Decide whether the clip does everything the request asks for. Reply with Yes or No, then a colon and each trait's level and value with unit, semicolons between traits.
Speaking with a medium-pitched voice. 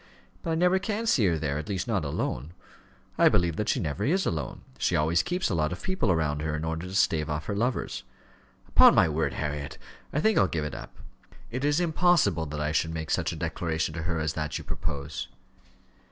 No: very low, 80 Hz